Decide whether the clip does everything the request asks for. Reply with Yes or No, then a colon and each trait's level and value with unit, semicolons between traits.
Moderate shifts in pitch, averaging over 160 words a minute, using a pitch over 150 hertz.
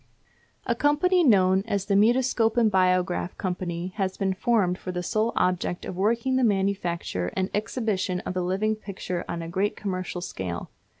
Yes: average, 3.4 semitones; average, 170 wpm; high, 190 Hz